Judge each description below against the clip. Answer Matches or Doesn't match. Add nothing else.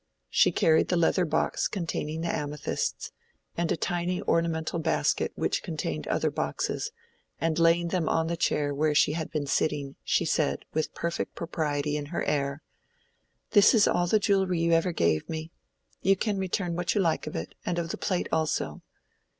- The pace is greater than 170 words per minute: Matches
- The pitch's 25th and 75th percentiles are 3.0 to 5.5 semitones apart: Doesn't match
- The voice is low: Doesn't match